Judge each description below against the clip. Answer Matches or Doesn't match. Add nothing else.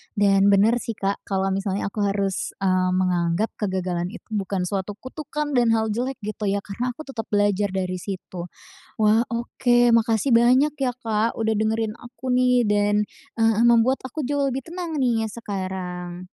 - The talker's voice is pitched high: Matches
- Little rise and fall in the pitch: Doesn't match